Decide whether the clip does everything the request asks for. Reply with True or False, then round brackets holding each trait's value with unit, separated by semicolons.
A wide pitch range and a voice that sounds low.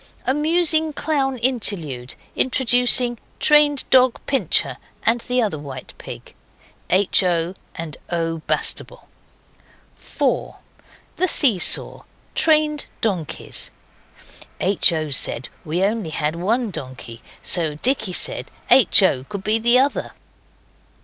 False (8.0 semitones; 220 Hz)